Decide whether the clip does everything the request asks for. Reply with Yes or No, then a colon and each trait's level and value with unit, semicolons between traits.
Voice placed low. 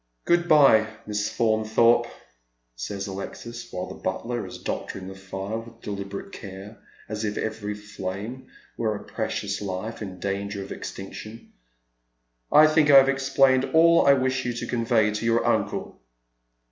Yes: low, 110 Hz